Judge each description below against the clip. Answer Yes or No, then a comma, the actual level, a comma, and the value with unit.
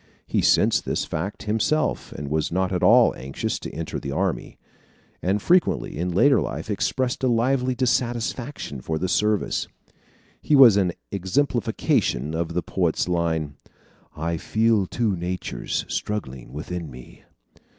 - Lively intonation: Yes, wide, 6.5 semitones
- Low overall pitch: Yes, very low, 95 Hz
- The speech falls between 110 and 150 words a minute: Yes, average, 140 wpm